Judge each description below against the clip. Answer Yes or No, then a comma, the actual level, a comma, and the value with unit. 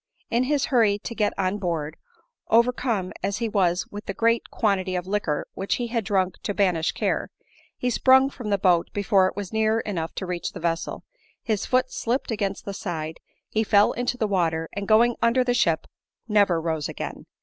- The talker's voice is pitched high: Yes, high, 205 Hz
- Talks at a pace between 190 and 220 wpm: Yes, average, 195 wpm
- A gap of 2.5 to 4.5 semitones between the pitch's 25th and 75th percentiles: Yes, average, 4.2 semitones